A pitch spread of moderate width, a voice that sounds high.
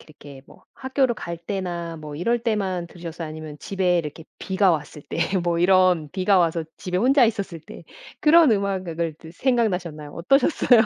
No: average, 3.9 semitones; medium, 180 Hz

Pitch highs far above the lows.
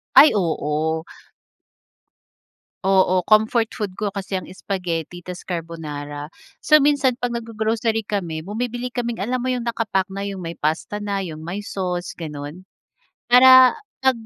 Yes: wide, 5.7 semitones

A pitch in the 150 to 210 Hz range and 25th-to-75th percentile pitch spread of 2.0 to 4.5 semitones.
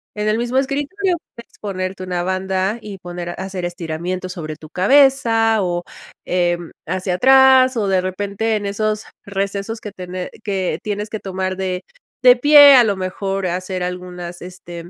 Yes: high, 190 Hz; average, 3.5 semitones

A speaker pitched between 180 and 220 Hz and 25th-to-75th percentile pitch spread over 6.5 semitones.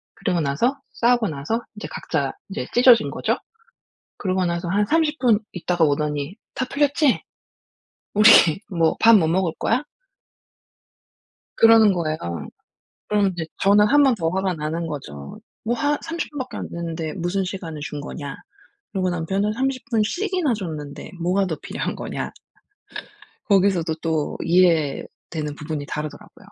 No: medium, 185 Hz; wide, 6.0 semitones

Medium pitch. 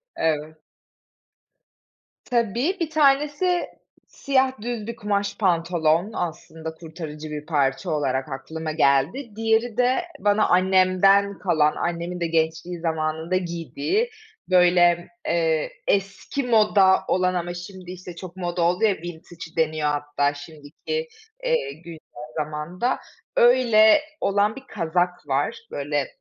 Yes: medium, 175 Hz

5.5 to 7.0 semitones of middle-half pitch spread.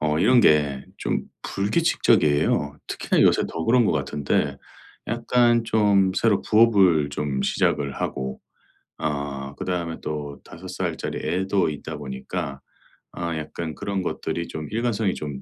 Yes: wide, 5.9 semitones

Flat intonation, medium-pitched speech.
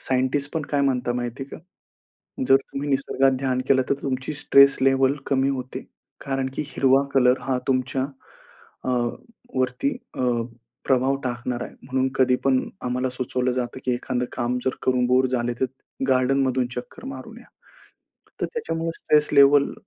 No: narrow, 1.4 semitones; low, 130 Hz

